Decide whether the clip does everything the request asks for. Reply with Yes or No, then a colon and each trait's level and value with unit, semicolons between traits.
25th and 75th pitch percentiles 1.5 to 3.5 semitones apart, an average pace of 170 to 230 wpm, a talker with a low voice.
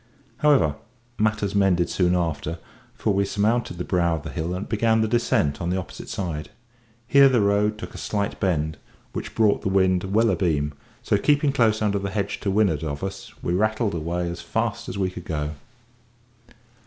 No: average, 4.0 semitones; average, 190 wpm; very low, 95 Hz